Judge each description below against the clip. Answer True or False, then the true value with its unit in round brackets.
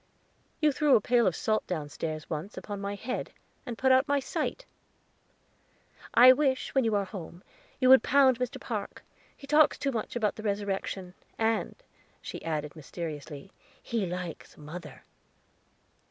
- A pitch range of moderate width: False (6.9 semitones)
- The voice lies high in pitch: True (210 Hz)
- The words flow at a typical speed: True (155 wpm)